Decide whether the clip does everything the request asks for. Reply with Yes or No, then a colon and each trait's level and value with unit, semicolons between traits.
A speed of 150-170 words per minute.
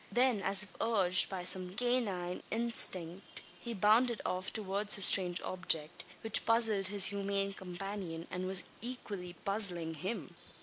No: average, 140 wpm